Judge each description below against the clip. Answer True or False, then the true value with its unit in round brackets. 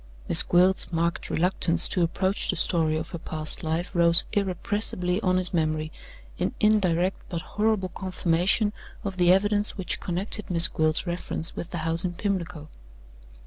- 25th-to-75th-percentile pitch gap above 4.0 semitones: False (2.5 semitones)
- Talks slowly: False (155 wpm)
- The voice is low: False (180 Hz)